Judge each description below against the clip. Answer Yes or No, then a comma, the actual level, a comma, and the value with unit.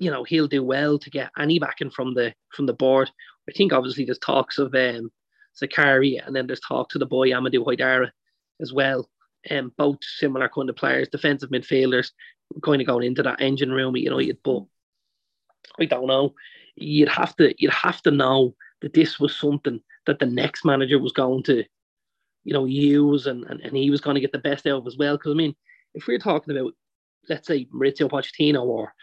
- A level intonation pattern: Yes, narrow, 2.0 semitones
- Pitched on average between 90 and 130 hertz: No, medium, 140 Hz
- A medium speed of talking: No, fast, 210 wpm